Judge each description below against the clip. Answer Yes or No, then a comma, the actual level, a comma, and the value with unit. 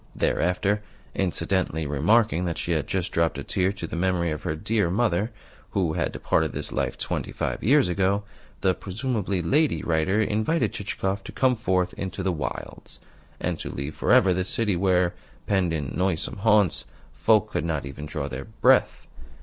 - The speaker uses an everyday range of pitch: Yes, average, 3.7 semitones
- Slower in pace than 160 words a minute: No, average, 175 wpm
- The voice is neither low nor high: No, very low, 95 Hz